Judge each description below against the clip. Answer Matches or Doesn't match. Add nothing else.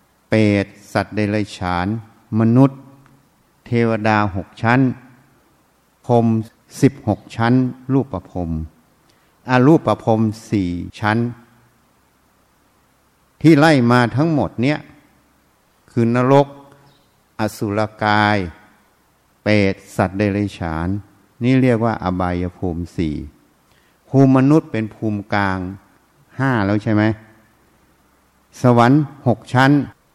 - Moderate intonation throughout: Matches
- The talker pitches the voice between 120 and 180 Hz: Doesn't match